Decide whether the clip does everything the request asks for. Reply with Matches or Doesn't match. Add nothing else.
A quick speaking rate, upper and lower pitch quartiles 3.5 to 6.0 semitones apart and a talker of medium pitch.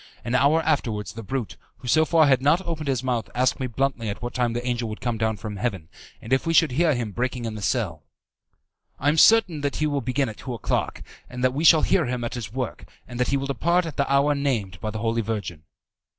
Doesn't match